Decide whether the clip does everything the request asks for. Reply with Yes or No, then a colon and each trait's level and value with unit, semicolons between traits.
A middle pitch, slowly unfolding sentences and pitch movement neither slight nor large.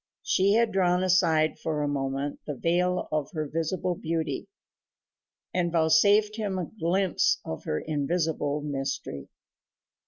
Yes: medium, 165 Hz; slow, 130 wpm; average, 3.8 semitones